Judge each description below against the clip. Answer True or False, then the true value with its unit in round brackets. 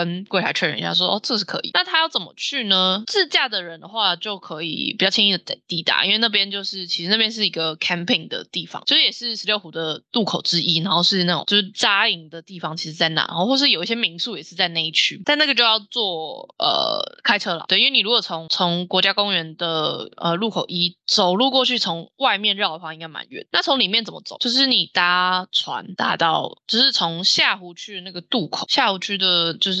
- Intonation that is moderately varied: True (4.8 semitones)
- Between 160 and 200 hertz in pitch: True (190 Hz)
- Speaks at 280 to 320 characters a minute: False (350 characters per minute)